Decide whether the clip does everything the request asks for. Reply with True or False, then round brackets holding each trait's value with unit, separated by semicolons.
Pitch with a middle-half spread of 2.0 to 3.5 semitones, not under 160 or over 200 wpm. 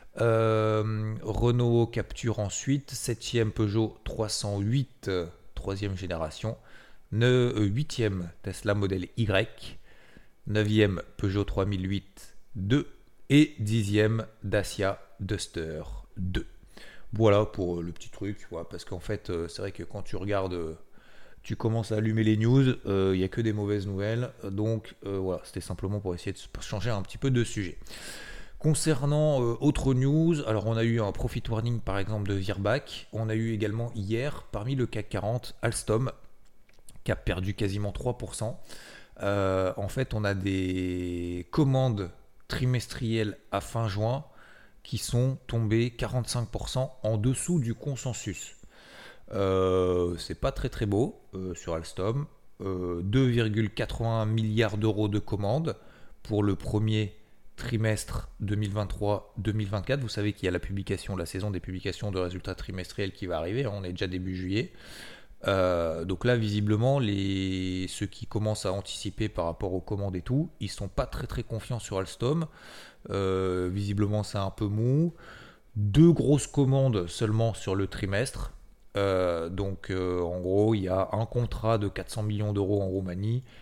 False (3.2 semitones; 150 wpm)